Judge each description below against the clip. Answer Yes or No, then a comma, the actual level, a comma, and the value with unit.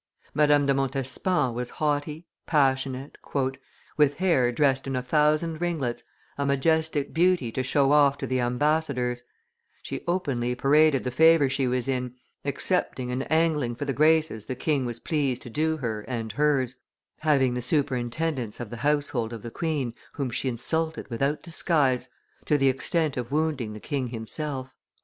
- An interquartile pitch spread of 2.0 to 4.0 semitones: Yes, average, 3.5 semitones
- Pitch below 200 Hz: Yes, low, 135 Hz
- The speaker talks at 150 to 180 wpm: Yes, average, 160 wpm